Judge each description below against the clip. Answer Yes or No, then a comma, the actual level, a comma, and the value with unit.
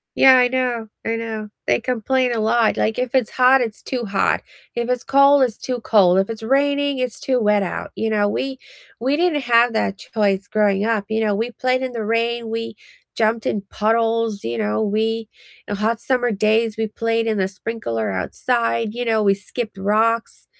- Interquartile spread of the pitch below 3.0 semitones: Yes, narrow, 2.6 semitones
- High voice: Yes, high, 225 Hz